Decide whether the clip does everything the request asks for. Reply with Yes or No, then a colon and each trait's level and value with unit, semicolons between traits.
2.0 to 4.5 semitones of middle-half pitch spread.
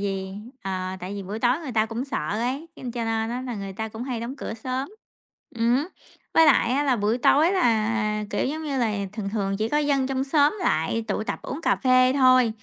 Yes: average, 3.9 semitones